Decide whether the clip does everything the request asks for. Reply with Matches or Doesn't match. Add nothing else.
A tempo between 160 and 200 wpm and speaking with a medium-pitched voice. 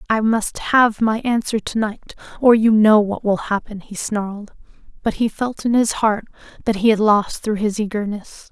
Doesn't match